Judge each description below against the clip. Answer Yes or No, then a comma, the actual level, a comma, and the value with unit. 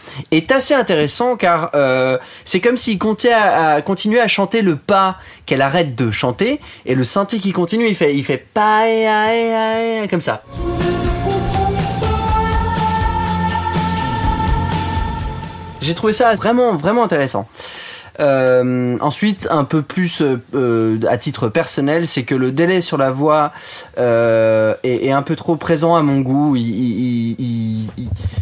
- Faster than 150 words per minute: No, slow, 145 wpm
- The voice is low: No, medium, 150 Hz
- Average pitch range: No, wide, 8.7 semitones